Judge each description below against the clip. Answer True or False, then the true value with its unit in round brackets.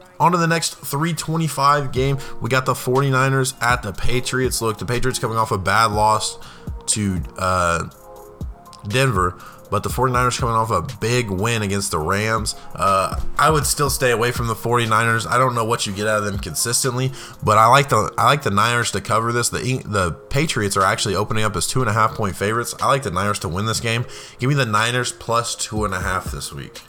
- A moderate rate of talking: False (220 wpm)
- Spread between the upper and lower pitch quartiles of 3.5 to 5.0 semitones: True (3.9 semitones)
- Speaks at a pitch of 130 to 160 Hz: False (115 Hz)